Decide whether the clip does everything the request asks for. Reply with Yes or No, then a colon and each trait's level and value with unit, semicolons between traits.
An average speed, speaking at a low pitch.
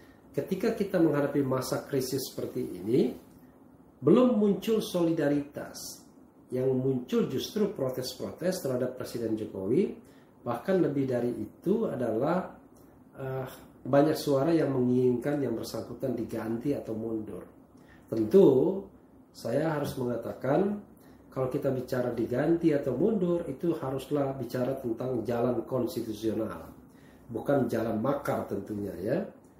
Yes: average, 105 wpm; low, 130 Hz